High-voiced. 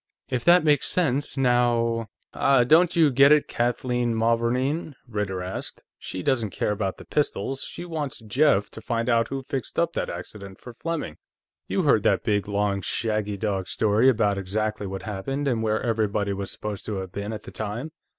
No: low, 115 Hz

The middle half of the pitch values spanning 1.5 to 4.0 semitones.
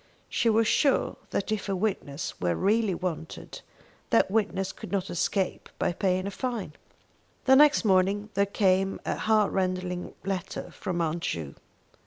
Yes: average, 2.9 semitones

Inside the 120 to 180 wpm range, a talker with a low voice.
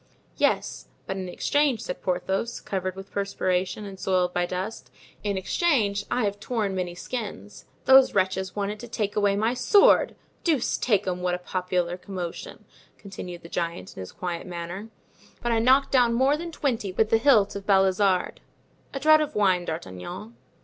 No: average, 170 wpm; high, 195 Hz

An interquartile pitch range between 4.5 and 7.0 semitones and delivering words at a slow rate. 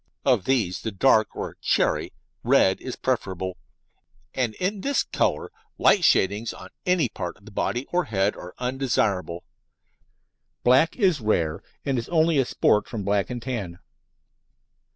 No: wide, 5.5 semitones; average, 150 wpm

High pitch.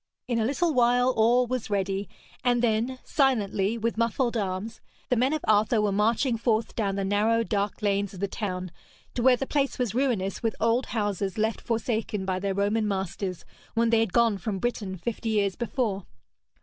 Yes: high, 220 Hz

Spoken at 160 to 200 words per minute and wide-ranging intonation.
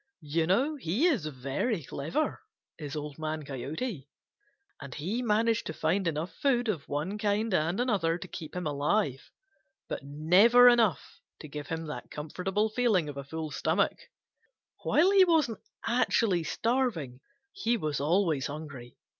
No: average, 150 wpm; wide, 7.2 semitones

